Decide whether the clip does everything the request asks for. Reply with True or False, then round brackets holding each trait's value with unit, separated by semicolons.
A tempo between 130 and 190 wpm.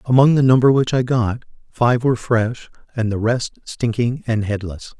True (180 wpm)